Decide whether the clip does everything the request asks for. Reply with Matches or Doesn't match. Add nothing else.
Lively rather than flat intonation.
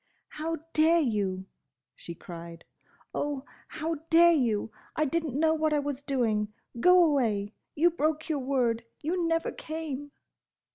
Matches